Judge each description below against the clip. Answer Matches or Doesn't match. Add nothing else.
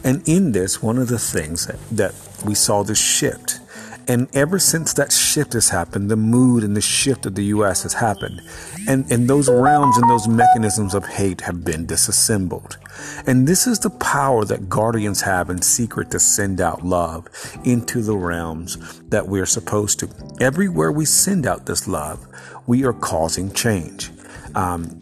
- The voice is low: Matches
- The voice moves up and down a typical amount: Doesn't match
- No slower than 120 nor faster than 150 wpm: Doesn't match